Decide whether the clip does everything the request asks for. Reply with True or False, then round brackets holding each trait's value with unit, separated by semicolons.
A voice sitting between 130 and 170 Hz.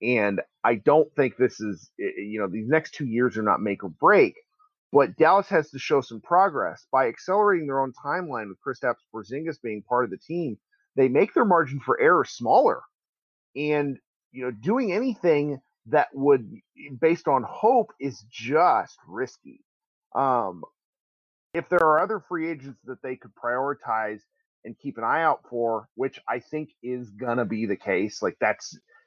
True (140 Hz)